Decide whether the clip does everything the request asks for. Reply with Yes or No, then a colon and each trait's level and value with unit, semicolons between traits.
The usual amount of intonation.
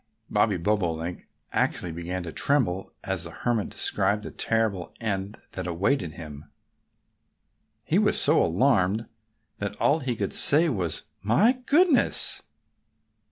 Yes: average, 4.9 semitones